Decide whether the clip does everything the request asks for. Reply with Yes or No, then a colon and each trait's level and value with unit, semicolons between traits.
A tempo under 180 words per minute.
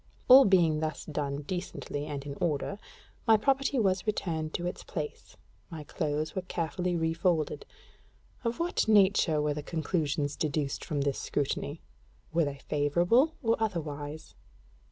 Yes: average, 140 wpm